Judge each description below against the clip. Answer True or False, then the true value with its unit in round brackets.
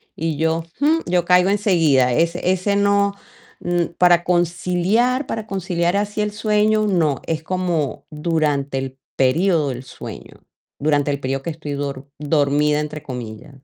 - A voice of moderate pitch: True (165 Hz)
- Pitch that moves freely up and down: False (4.9 semitones)